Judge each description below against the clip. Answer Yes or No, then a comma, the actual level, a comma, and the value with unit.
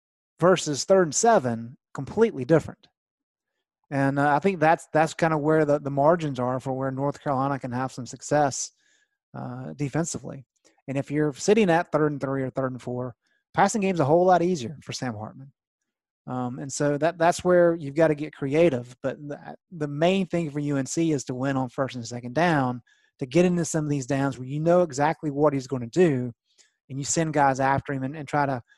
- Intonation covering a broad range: No, average, 3.6 semitones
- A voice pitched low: No, medium, 145 Hz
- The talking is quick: Yes, fast, 215 wpm